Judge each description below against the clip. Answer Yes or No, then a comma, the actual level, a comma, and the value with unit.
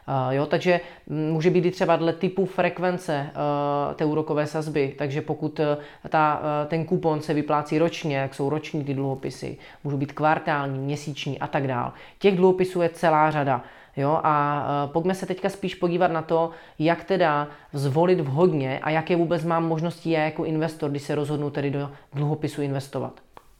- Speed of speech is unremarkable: No, fast, 175 wpm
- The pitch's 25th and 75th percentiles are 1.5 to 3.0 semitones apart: Yes, narrow, 2.6 semitones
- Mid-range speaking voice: Yes, medium, 155 Hz